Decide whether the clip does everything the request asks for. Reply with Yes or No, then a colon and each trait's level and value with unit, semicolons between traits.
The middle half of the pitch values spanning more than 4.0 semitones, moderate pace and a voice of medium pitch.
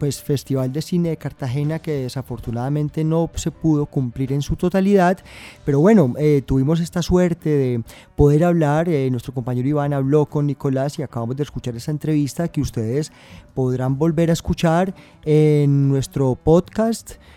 No: average, 3.3 semitones; average, 160 wpm; medium, 145 Hz